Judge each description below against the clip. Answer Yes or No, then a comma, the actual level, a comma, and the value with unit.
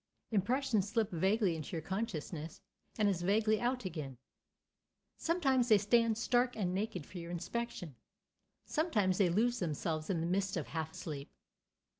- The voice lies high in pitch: Yes, high, 195 Hz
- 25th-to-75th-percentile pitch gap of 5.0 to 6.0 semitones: Yes, wide, 5.4 semitones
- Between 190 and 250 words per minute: No, average, 150 wpm